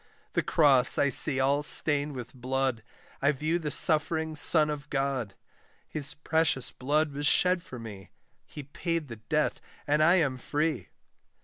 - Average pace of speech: Yes, average, 155 wpm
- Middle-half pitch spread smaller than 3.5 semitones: Yes, average, 2.8 semitones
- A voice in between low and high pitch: Yes, medium, 145 Hz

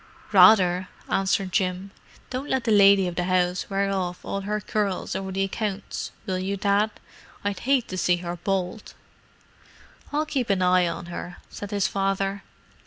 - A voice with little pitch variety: Yes, narrow, 1.9 semitones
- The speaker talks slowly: No, average, 170 wpm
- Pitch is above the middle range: Yes, high, 195 Hz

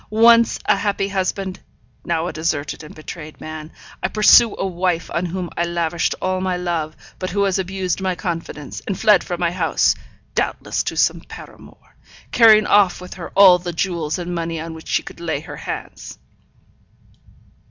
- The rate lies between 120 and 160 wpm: No, average, 175 wpm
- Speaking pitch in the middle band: Yes, medium, 180 Hz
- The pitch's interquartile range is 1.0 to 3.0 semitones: Yes, narrow, 2.5 semitones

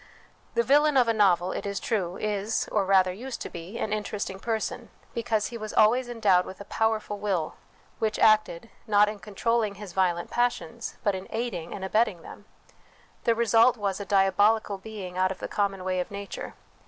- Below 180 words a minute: No, average, 190 wpm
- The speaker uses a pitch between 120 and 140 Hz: No, high, 205 Hz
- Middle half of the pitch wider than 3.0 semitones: No, average, 2.7 semitones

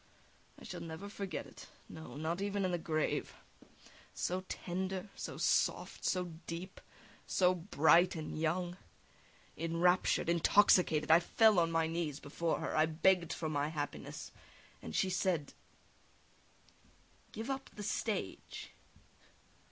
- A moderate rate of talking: No, slow, 130 wpm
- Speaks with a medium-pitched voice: Yes, medium, 170 Hz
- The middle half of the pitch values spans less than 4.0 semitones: Yes, average, 2.8 semitones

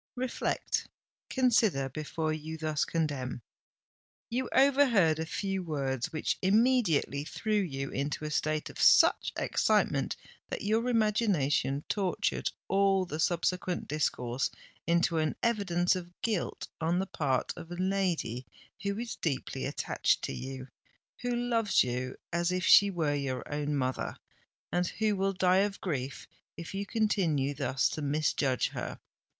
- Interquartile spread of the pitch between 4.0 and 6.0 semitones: Yes, wide, 5.6 semitones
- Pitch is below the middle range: No, medium, 170 Hz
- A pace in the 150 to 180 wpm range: No, slow, 135 wpm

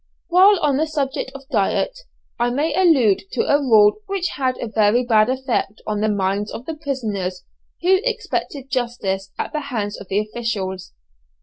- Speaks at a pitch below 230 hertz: No, high, 245 Hz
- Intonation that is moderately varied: No, wide, 5.8 semitones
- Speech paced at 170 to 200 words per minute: Yes, average, 175 wpm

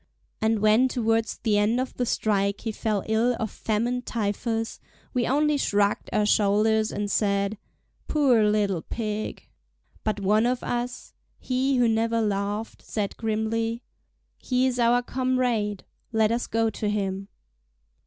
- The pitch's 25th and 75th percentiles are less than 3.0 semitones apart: Yes, narrow, 2.6 semitones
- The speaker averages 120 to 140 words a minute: Yes, slow, 135 wpm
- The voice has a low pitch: No, high, 220 Hz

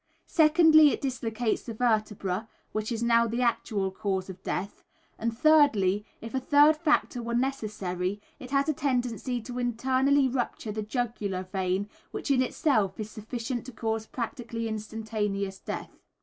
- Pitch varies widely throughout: No, average, 3.7 semitones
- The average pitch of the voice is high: Yes, high, 230 Hz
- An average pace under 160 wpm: Yes, average, 150 wpm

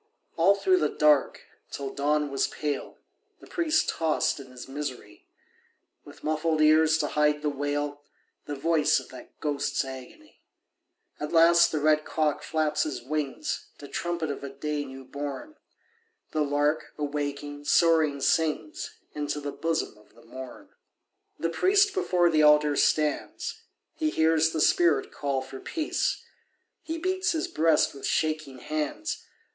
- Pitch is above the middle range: No, medium, 150 Hz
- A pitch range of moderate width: No, narrow, 2.1 semitones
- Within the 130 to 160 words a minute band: Yes, average, 150 wpm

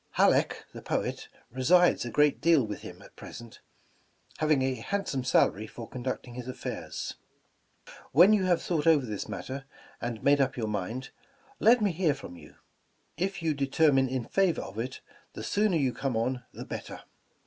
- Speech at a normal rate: Yes, average, 170 wpm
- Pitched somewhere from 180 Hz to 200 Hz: No, low, 135 Hz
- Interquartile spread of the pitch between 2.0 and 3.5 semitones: No, average, 5.3 semitones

